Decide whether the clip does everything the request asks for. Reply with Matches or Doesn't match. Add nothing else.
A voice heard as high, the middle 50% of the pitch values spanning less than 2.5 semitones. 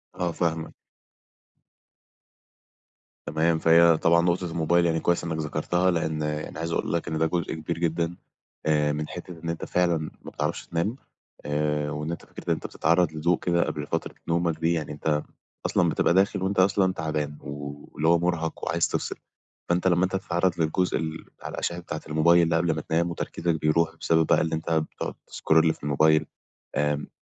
Doesn't match